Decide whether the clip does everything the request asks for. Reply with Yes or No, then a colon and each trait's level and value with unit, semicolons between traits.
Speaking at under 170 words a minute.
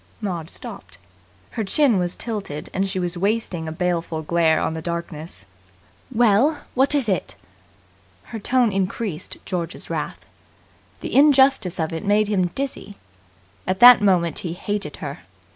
Yes: average, 145 wpm